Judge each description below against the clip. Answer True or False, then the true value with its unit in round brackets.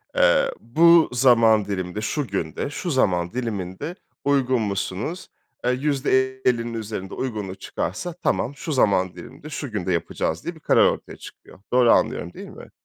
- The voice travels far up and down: True (6.6 semitones)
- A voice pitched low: True (120 Hz)